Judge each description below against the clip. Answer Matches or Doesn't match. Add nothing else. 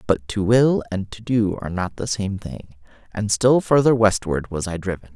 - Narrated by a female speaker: Doesn't match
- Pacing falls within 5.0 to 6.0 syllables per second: Doesn't match